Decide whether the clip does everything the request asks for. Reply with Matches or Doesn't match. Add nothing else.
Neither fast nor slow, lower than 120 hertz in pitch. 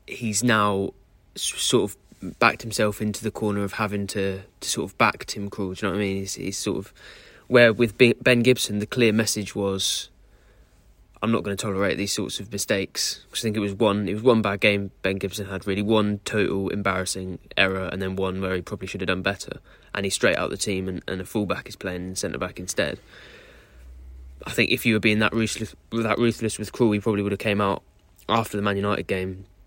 Doesn't match